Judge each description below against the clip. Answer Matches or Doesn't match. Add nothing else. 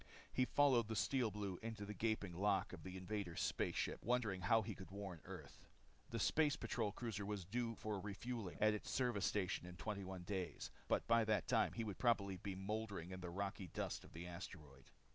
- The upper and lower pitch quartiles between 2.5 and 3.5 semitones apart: Matches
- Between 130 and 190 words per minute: Doesn't match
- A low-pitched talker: Matches